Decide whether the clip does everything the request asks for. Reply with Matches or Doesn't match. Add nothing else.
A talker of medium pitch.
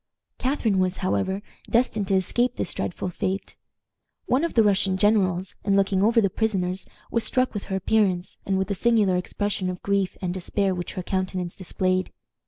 Doesn't match